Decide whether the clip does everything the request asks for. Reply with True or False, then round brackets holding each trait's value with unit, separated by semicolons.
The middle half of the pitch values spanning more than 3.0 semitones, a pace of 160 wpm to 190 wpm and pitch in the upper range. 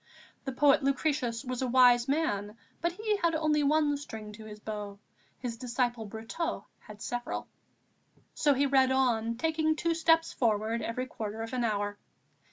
True (5.1 semitones; 165 wpm; 250 Hz)